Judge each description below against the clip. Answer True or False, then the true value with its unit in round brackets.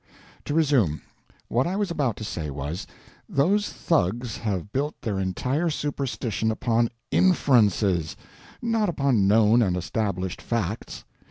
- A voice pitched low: True (115 Hz)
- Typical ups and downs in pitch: False (7.1 semitones)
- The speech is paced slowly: True (125 wpm)